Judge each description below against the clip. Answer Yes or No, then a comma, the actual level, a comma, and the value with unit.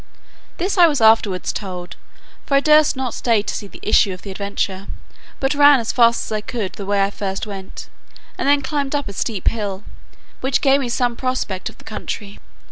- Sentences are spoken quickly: Yes, fast, 210 wpm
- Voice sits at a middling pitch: No, high, 225 Hz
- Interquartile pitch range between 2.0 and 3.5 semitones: No, average, 5.2 semitones